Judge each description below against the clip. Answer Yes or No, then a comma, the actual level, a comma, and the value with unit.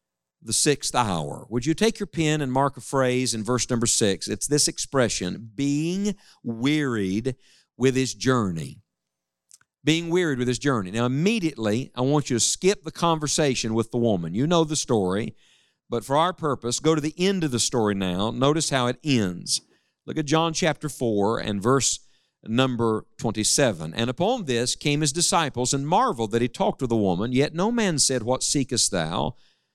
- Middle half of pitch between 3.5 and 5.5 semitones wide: Yes, average, 5.0 semitones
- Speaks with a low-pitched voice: Yes, low, 130 Hz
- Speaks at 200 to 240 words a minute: No, average, 185 wpm